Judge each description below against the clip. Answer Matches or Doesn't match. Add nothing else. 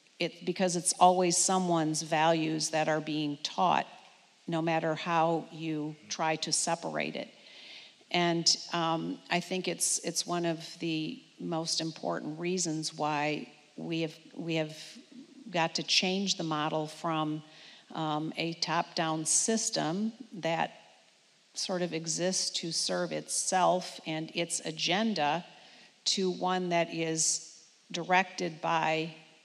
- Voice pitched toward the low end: Doesn't match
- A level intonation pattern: Matches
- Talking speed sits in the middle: Doesn't match